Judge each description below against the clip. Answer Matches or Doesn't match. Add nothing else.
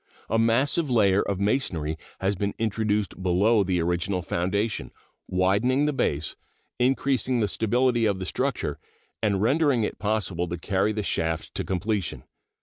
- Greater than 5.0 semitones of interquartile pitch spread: Doesn't match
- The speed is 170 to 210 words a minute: Doesn't match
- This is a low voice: Matches